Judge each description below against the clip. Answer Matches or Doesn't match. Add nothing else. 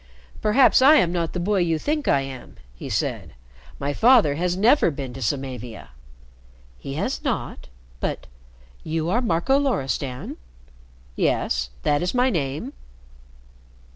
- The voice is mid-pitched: Matches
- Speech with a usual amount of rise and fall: Doesn't match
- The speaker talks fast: Doesn't match